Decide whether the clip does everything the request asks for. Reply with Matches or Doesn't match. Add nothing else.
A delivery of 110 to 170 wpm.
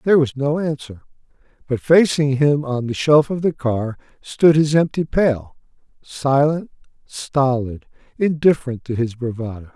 Matches